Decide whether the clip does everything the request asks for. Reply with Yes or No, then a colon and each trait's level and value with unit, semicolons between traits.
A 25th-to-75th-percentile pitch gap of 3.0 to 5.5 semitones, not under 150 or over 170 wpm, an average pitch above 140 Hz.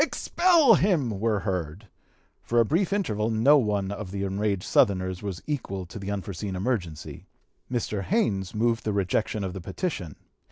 No: average, 3.9 semitones; average, 160 wpm; low, 105 Hz